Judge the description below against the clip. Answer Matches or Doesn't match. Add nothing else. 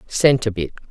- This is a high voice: Doesn't match